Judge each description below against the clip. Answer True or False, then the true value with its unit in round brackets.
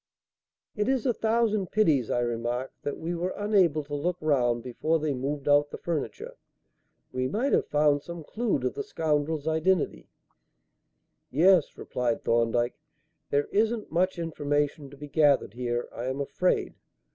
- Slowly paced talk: False (155 wpm)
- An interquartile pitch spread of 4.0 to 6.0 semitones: True (5.2 semitones)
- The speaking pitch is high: False (150 Hz)